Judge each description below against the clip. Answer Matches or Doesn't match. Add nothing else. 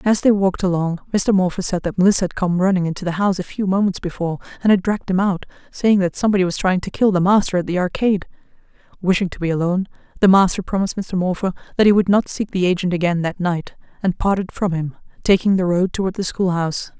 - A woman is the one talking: Matches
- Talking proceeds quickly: Matches